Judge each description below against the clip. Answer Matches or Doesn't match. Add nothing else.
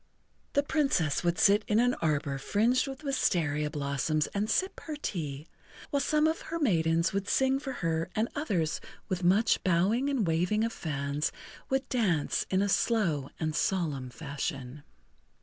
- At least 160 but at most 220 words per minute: Matches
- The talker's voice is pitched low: Doesn't match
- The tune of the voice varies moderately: Doesn't match